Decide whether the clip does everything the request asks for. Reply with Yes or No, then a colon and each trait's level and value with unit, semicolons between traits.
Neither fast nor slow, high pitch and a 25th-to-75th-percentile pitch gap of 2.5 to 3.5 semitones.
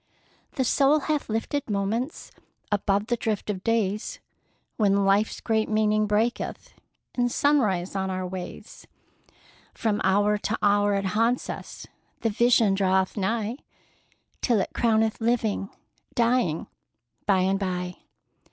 No: slow, 125 wpm; high, 210 Hz; average, 2.9 semitones